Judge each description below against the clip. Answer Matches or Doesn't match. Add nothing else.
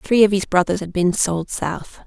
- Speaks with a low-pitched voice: Doesn't match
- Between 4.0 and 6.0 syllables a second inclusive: Matches